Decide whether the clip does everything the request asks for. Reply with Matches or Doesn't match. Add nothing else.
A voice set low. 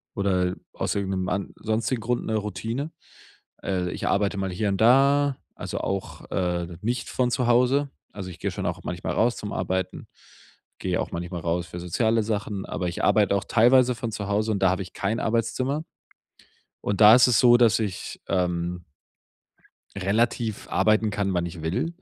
Matches